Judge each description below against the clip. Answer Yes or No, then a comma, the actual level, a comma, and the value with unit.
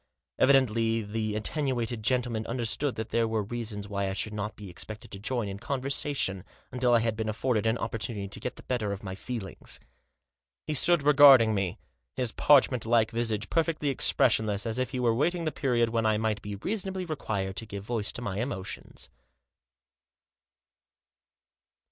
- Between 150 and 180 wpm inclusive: Yes, average, 170 wpm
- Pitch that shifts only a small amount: No, average, 3.3 semitones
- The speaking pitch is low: Yes, low, 115 Hz